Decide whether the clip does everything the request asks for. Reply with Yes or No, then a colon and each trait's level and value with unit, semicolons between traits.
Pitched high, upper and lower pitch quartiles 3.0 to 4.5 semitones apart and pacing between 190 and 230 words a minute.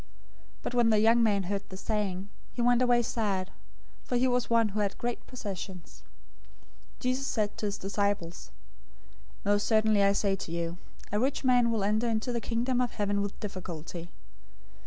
No: high, 210 Hz; average, 3.3 semitones; average, 180 wpm